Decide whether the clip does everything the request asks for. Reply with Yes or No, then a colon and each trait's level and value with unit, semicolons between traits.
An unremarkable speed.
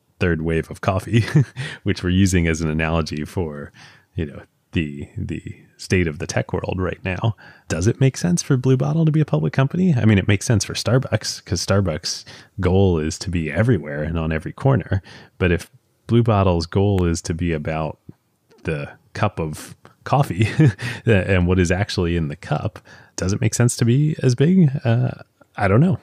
Yes: average, 195 wpm